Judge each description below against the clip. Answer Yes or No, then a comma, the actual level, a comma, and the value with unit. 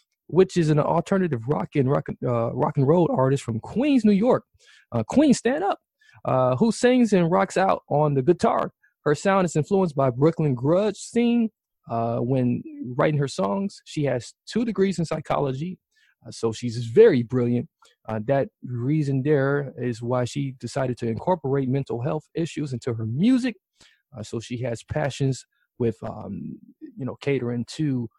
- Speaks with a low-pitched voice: No, medium, 145 Hz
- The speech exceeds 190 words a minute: No, average, 170 wpm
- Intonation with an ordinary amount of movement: No, wide, 7.5 semitones